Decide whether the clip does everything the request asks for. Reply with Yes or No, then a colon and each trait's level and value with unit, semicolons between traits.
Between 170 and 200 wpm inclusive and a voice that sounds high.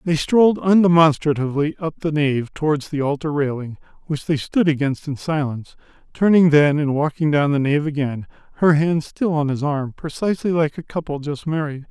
No: average, 180 wpm; medium, 150 Hz